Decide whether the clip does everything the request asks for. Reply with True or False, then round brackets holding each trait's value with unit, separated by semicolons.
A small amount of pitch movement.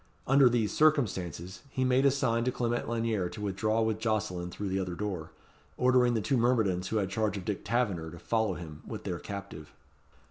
False (4.4 semitones)